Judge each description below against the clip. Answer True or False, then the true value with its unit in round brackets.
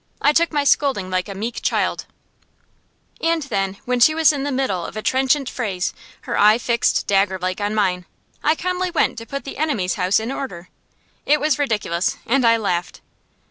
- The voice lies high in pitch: True (230 Hz)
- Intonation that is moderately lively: False (6.7 semitones)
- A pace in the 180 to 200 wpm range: True (185 wpm)